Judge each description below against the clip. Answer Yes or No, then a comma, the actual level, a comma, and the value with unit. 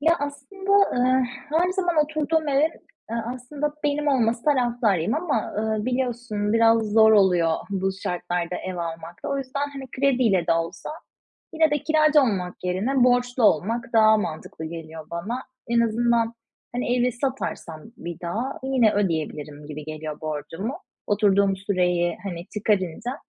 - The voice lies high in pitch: Yes, high, 225 Hz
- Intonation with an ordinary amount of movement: No, wide, 6.9 semitones